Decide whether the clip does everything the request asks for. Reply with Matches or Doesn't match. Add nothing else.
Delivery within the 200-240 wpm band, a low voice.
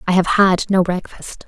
Doesn't match